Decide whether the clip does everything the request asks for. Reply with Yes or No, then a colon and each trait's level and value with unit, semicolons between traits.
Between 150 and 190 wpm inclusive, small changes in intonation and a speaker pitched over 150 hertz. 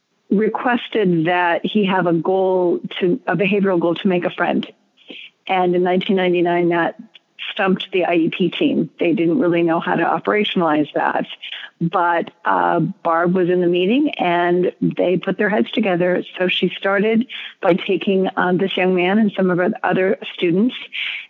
Yes: average, 165 wpm; narrow, 2.3 semitones; medium, 185 Hz